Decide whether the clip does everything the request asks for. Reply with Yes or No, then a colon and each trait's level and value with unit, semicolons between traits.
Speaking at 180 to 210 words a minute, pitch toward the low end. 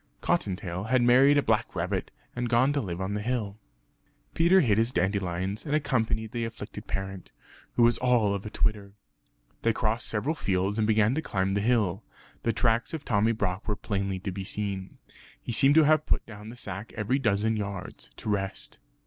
Yes: average, 190 wpm; low, 110 Hz